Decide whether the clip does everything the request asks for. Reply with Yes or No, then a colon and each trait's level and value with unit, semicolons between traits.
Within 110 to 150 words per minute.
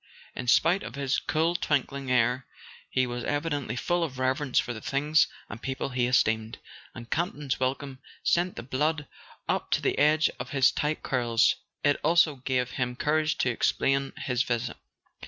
No: average, 170 wpm